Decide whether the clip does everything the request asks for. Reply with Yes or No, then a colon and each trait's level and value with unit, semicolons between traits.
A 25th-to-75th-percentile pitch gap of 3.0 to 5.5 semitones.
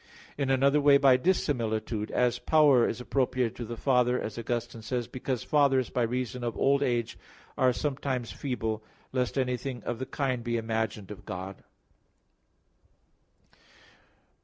No: narrow, 2.6 semitones